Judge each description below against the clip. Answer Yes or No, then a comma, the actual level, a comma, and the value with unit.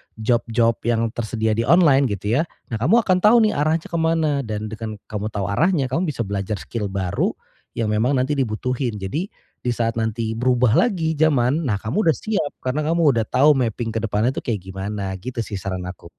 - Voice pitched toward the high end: No, low, 120 Hz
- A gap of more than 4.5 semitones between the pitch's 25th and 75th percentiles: Yes, wide, 5.5 semitones